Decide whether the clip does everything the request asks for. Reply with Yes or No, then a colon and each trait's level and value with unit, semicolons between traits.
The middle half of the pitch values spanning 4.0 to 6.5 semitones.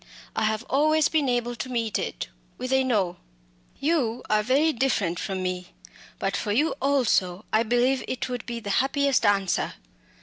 Yes: average, 4.6 semitones